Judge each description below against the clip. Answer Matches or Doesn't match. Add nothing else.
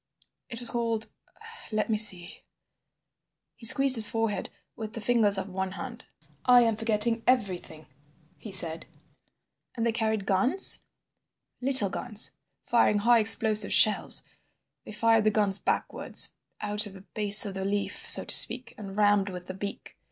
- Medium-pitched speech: Doesn't match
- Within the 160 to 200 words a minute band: Doesn't match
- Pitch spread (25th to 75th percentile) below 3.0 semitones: Matches